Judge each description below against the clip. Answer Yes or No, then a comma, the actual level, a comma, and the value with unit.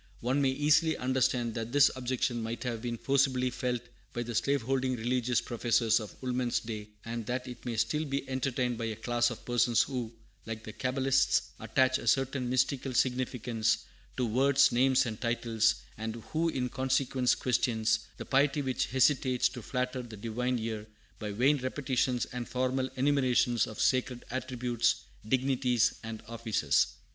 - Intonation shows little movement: Yes, narrow, 2.1 semitones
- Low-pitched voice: Yes, low, 125 Hz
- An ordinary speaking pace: Yes, average, 160 wpm